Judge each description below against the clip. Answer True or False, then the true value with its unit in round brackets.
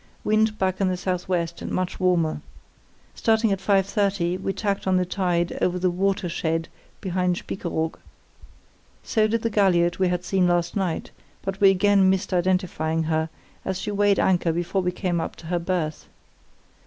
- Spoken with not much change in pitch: True (2.0 semitones)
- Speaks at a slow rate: False (165 wpm)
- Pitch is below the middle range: False (185 Hz)